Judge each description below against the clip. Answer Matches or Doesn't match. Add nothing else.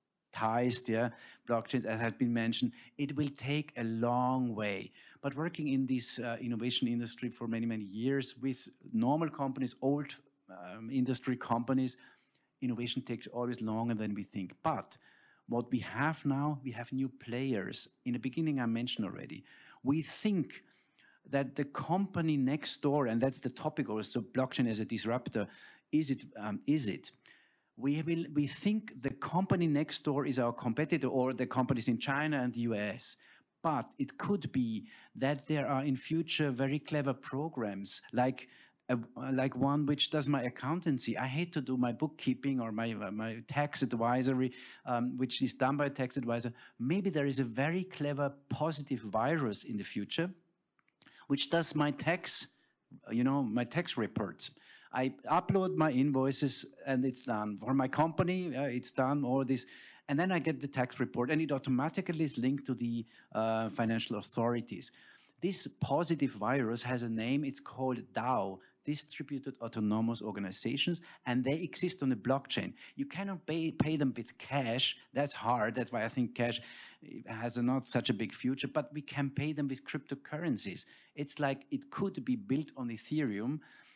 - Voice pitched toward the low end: Matches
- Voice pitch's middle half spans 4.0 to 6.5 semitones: Doesn't match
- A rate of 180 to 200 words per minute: Doesn't match